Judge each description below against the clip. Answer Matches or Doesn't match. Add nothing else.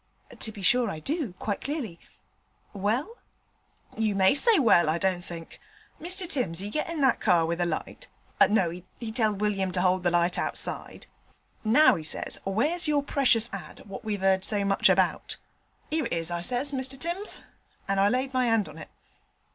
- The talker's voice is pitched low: Doesn't match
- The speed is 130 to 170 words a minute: Doesn't match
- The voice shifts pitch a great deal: Matches